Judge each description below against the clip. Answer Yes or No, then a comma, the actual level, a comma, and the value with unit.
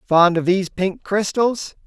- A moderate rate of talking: Yes, average, 160 wpm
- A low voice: No, high, 190 Hz